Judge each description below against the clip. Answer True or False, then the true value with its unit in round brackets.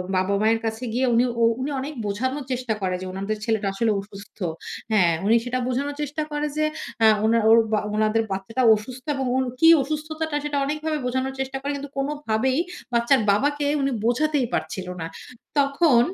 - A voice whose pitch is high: True (255 Hz)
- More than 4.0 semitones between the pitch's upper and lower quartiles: True (4.7 semitones)